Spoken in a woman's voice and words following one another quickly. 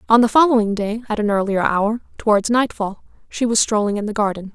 Yes: female; fast, 210 wpm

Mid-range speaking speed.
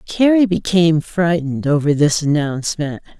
No: slow, 115 wpm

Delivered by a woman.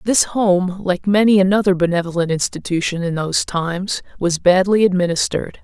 Yes: female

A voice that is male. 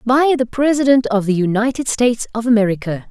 No: female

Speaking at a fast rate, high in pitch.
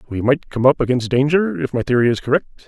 No: fast, 245 wpm; low, 135 Hz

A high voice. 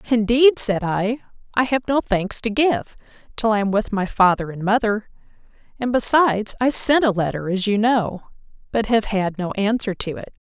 Yes: high, 220 Hz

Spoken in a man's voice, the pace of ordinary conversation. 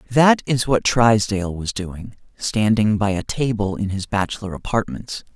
Yes: male; average, 155 wpm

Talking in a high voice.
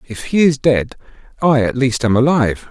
No: low, 125 Hz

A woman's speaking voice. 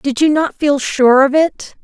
Yes: female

